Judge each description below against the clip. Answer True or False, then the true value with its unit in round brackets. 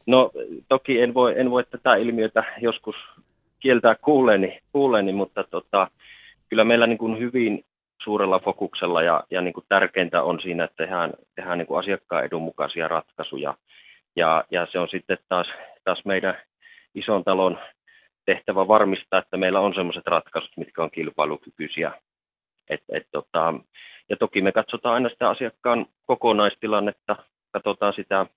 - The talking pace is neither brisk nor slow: True (145 wpm)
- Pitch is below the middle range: True (115 Hz)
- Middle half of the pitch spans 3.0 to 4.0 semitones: True (3.5 semitones)